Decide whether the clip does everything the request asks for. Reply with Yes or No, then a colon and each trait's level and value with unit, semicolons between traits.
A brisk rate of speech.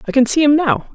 Yes: fast, 320 wpm